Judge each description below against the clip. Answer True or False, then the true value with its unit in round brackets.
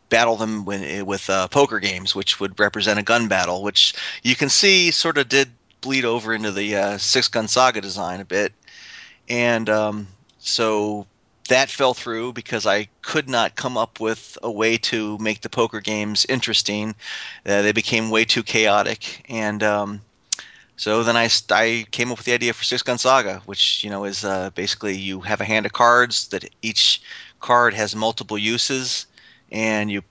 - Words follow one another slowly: False (185 wpm)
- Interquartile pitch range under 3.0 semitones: True (2.6 semitones)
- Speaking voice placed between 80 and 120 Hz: True (110 Hz)